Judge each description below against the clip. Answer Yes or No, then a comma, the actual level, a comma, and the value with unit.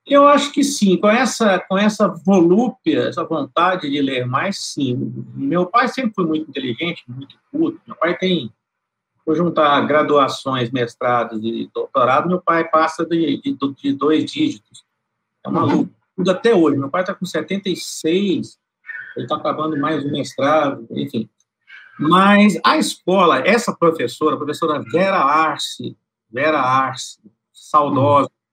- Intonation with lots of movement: Yes, wide, 6.4 semitones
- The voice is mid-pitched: Yes, medium, 170 Hz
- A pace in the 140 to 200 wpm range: Yes, average, 145 wpm